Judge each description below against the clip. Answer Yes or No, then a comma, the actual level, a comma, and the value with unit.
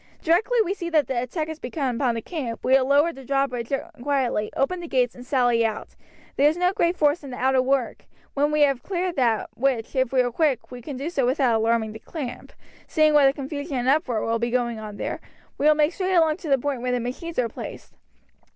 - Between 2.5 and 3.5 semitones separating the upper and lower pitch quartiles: No, average, 3.9 semitones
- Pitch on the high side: Yes, very high, 270 Hz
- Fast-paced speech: Yes, fast, 235 wpm